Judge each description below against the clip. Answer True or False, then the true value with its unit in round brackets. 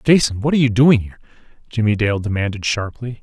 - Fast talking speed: False (185 wpm)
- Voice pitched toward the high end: False (115 Hz)